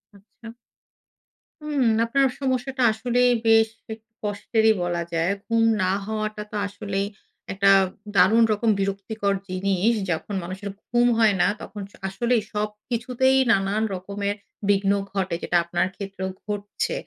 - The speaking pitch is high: Yes, high, 210 Hz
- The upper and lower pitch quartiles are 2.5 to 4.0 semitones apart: Yes, average, 2.8 semitones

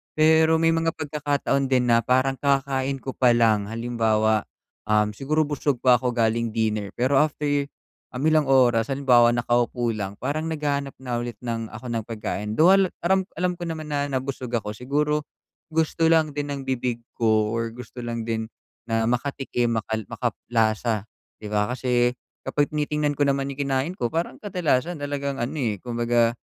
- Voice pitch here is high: No, low, 130 Hz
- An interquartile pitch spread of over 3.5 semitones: Yes, average, 3.9 semitones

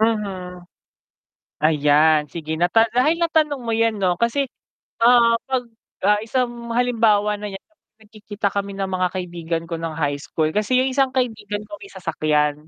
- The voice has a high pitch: Yes, high, 210 Hz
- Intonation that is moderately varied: No, wide, 5.8 semitones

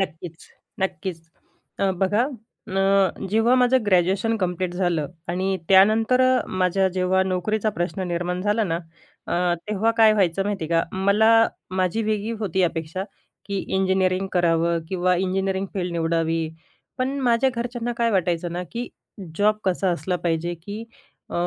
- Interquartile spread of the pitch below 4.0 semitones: Yes, average, 3.3 semitones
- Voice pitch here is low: No, high, 190 Hz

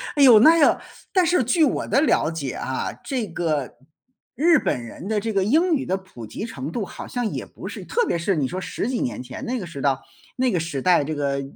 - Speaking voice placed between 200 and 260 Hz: No, high, 190 Hz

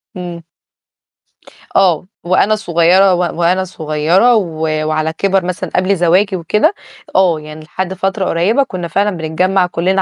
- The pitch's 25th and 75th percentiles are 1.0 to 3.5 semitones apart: Yes, narrow, 2.5 semitones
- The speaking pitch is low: No, medium, 180 Hz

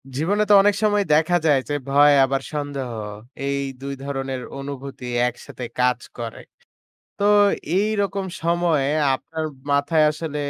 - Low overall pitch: No, medium, 145 Hz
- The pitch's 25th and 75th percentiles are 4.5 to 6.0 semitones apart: No, average, 4.1 semitones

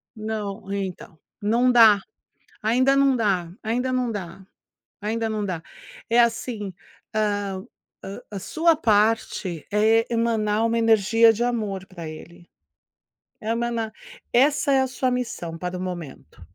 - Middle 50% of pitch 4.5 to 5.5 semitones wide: No, average, 3.4 semitones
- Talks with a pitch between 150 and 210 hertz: No, high, 220 Hz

